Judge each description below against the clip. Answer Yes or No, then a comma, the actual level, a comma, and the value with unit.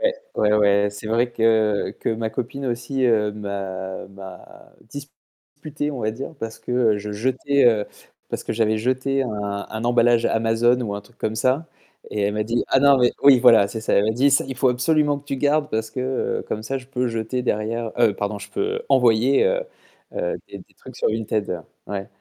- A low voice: Yes, low, 115 Hz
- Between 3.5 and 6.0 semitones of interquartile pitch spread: Yes, average, 3.9 semitones